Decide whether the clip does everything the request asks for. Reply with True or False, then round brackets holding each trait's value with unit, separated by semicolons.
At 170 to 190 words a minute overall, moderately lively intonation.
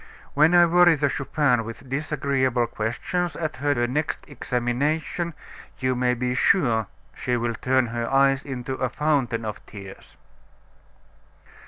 False (135 wpm; 3.7 semitones)